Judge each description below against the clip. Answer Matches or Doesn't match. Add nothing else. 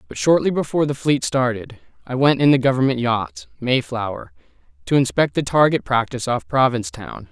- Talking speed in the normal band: Matches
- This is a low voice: Matches